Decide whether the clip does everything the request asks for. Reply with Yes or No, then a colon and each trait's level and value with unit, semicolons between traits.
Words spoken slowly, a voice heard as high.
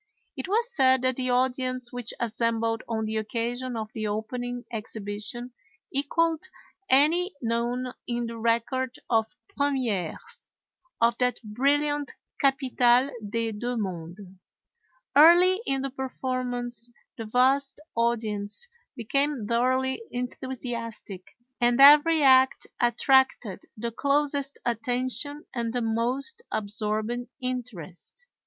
Yes: slow, 110 wpm; high, 245 Hz